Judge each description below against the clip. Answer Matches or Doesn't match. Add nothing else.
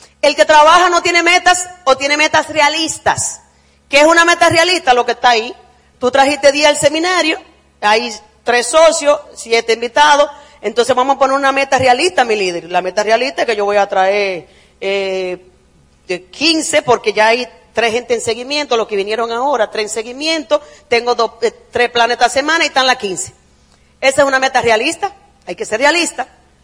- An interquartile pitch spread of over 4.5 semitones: Matches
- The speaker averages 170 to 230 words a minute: Matches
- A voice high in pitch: Matches